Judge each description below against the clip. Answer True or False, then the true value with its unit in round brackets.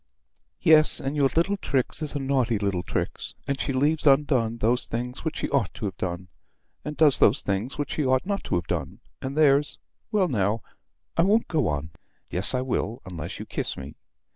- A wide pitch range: True (6.4 semitones)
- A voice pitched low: True (130 Hz)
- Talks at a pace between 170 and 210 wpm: True (200 wpm)